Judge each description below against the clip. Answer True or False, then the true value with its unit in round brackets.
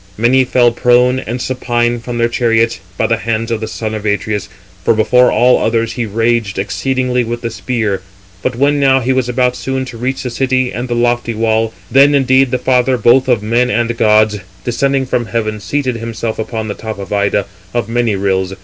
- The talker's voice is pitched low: True (120 Hz)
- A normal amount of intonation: False (2.3 semitones)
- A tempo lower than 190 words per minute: False (205 wpm)